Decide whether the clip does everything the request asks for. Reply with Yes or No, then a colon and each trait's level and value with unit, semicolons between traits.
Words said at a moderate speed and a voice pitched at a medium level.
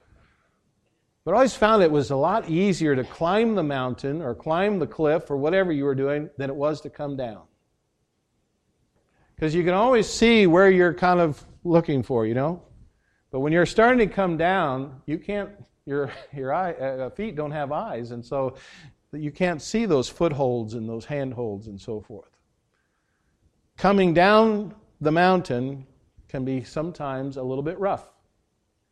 Yes: average, 170 wpm; medium, 150 Hz